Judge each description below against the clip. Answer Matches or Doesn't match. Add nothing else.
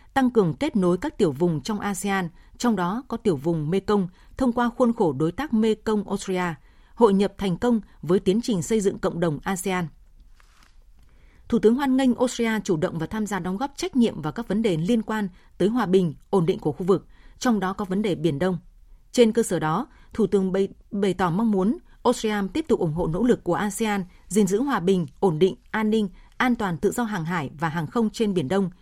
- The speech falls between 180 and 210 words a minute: Doesn't match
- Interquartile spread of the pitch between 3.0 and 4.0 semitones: Matches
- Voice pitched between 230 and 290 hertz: Doesn't match